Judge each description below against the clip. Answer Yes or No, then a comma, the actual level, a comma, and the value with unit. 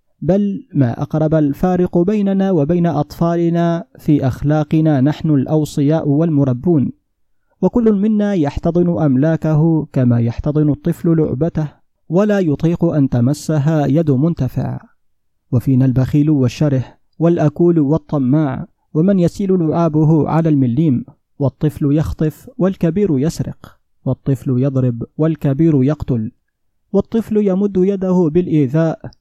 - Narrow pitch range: No, average, 3.3 semitones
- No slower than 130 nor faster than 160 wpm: No, average, 100 wpm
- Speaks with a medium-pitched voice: Yes, medium, 155 Hz